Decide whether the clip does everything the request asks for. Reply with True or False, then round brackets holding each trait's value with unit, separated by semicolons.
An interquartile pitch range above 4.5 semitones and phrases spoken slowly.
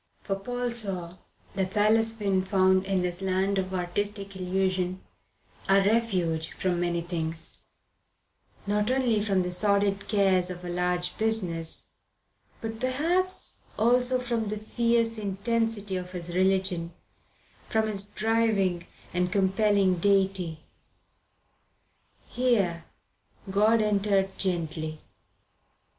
False (3.3 semitones; 110 wpm)